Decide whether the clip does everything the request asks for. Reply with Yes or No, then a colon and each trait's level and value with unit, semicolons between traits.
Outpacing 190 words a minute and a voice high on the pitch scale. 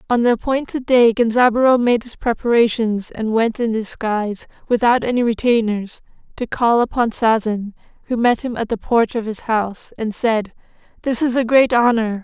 No: average, 170 wpm; high, 230 Hz